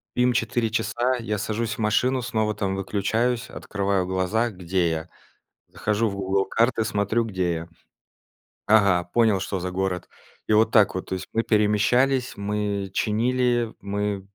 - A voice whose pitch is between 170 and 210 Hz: No, low, 105 Hz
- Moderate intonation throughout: Yes, average, 3.0 semitones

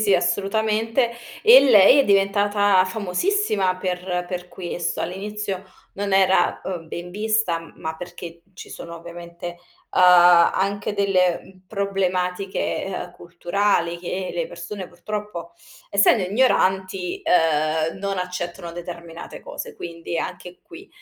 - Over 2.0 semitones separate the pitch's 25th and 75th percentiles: Yes, average, 2.7 semitones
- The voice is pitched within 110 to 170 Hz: No, medium, 185 Hz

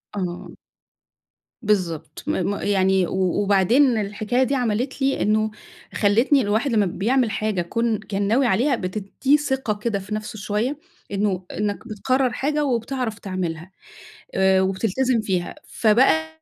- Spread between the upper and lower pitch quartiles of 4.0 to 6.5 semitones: Yes, average, 4.5 semitones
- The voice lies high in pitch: Yes, high, 210 Hz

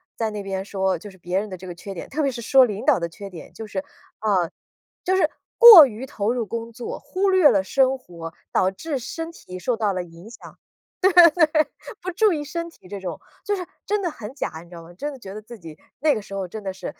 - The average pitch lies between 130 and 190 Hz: No, high, 215 Hz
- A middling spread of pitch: No, wide, 6.9 semitones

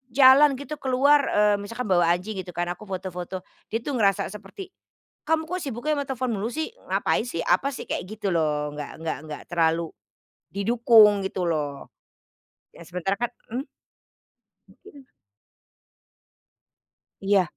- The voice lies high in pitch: Yes, high, 210 Hz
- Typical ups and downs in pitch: No, wide, 6.9 semitones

